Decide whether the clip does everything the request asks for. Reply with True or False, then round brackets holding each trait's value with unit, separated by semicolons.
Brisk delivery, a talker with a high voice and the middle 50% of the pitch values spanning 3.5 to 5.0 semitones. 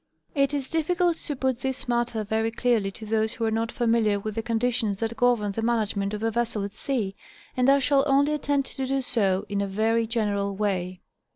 True (210 wpm; 230 Hz; 3.9 semitones)